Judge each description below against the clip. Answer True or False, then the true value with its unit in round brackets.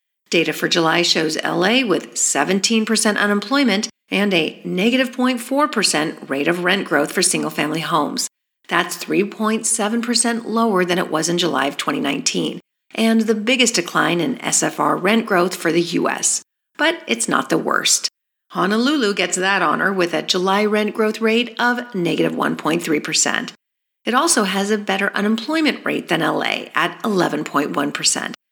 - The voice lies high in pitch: True (205 Hz)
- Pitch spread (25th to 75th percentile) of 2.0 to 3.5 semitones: False (4.4 semitones)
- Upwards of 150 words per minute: False (145 wpm)